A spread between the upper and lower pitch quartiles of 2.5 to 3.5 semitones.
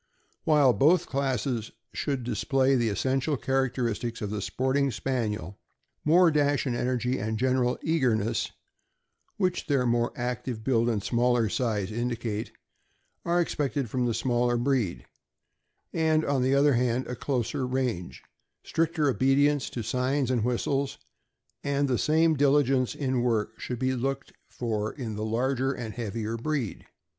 Yes: average, 2.9 semitones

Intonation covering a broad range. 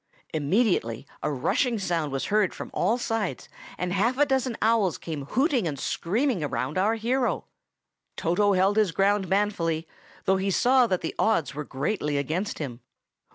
Yes: wide, 6.2 semitones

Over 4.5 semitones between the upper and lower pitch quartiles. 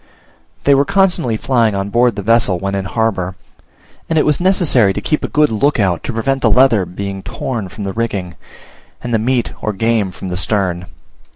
Yes: average, 5.1 semitones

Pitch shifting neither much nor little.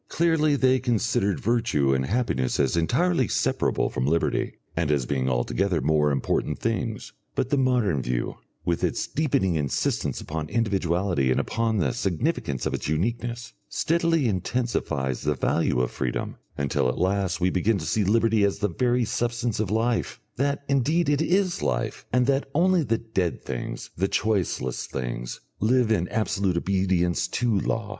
No: wide, 7.6 semitones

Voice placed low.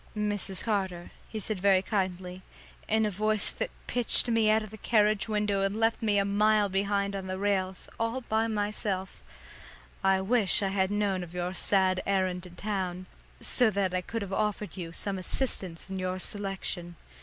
No: high, 200 Hz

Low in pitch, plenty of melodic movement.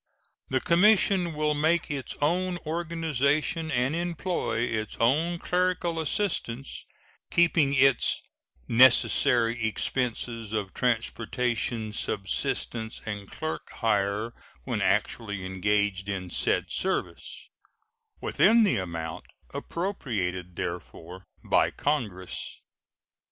Yes: low, 125 Hz; wide, 7.8 semitones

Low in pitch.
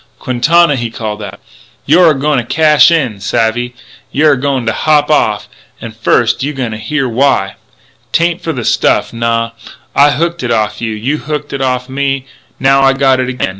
Yes: low, 130 Hz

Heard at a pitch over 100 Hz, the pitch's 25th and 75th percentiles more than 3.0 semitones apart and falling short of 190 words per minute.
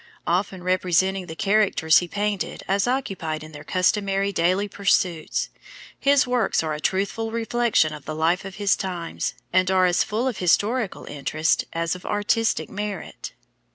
Yes: high, 190 Hz; average, 3.6 semitones; average, 155 wpm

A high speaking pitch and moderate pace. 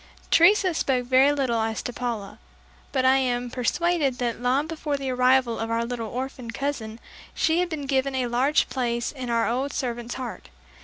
Yes: very high, 255 Hz; average, 185 wpm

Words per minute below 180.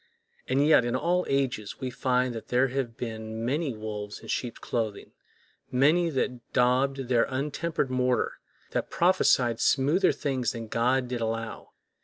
Yes: average, 150 wpm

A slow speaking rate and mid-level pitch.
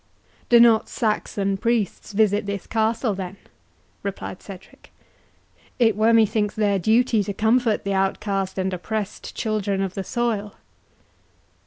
No: slow, 130 wpm; high, 210 Hz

